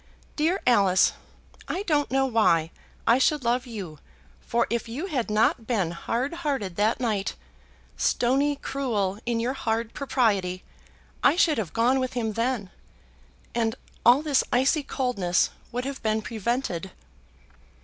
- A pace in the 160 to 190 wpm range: No, average, 140 wpm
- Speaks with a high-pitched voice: Yes, high, 235 Hz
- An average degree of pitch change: Yes, average, 4.1 semitones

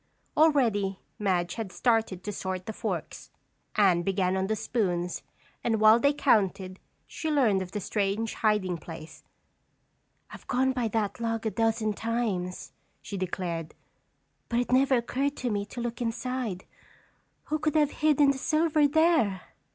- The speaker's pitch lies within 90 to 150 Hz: No, high, 220 Hz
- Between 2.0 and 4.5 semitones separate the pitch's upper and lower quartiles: No, average, 5.0 semitones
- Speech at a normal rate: Yes, average, 150 wpm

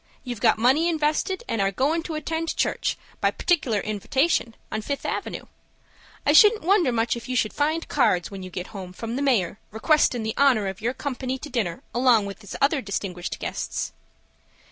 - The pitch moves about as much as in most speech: No, wide, 6.0 semitones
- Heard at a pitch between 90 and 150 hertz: No, very high, 250 Hz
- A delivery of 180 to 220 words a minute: Yes, average, 185 wpm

